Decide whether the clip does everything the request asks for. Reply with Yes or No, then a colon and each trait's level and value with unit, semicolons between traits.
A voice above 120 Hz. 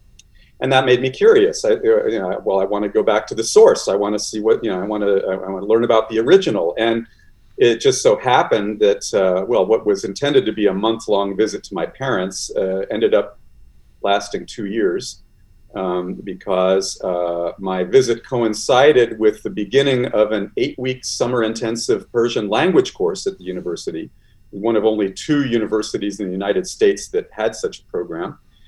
No: low, 115 Hz